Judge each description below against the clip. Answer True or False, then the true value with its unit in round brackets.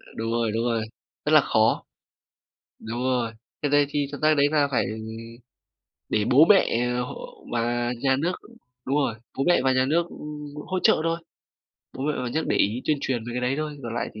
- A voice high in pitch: False (135 Hz)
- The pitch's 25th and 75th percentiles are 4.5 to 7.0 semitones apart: False (3.9 semitones)